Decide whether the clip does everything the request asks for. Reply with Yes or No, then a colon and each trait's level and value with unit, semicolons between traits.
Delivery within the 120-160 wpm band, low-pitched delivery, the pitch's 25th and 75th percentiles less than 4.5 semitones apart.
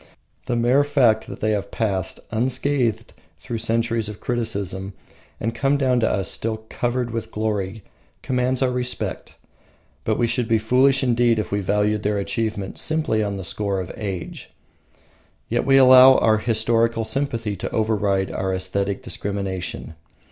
Yes: average, 155 wpm; low, 110 Hz; average, 3.4 semitones